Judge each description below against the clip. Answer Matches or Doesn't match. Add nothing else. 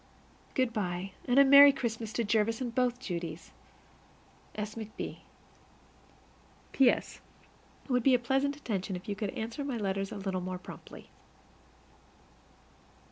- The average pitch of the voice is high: Matches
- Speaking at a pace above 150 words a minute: Doesn't match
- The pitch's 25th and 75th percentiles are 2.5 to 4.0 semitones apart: Doesn't match